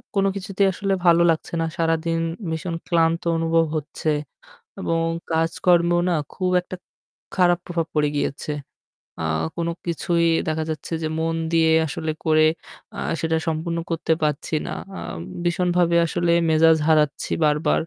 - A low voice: No, medium, 165 Hz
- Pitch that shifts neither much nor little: No, narrow, 1.4 semitones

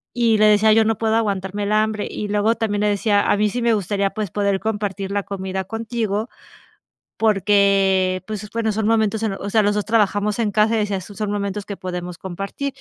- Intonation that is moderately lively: No, narrow, 1.7 semitones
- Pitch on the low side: No, high, 205 Hz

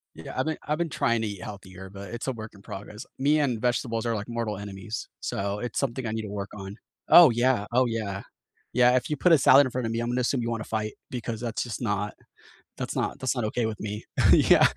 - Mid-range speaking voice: No, low, 115 Hz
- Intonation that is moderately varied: Yes, average, 3.2 semitones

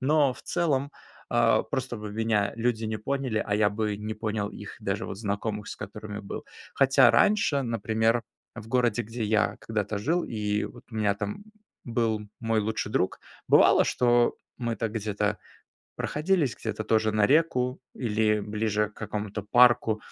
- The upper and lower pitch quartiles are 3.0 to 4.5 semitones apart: No, narrow, 2.4 semitones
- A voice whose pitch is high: No, low, 110 Hz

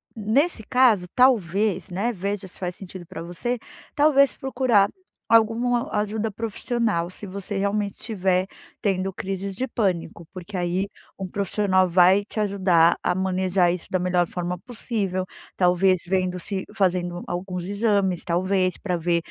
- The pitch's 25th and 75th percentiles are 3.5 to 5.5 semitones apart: No, average, 2.9 semitones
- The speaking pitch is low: No, high, 190 Hz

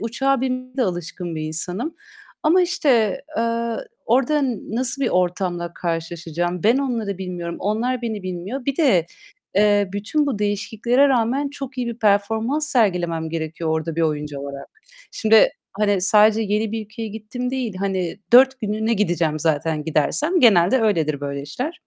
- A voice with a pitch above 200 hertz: Yes, high, 210 Hz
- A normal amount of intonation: No, wide, 6.3 semitones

